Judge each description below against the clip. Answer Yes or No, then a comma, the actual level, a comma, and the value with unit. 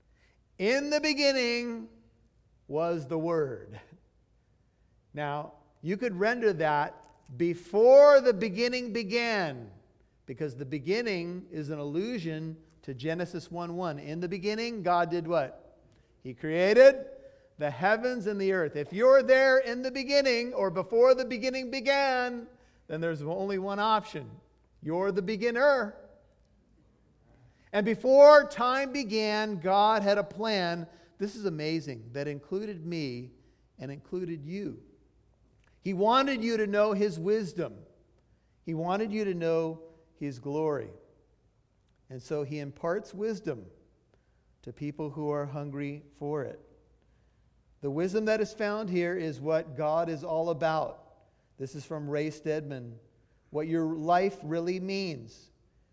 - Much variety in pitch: Yes, wide, 6.5 semitones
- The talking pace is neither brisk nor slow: No, slow, 130 wpm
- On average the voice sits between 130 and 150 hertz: No, medium, 175 Hz